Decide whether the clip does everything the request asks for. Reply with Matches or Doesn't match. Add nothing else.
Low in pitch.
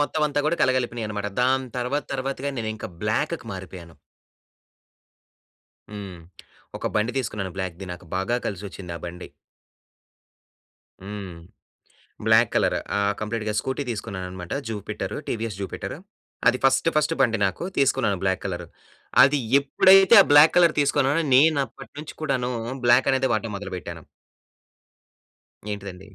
Matches